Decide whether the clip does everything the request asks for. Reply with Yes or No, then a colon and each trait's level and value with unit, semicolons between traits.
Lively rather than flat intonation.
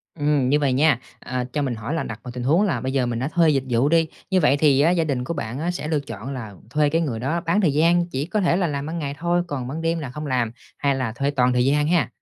No: average, 4.3 semitones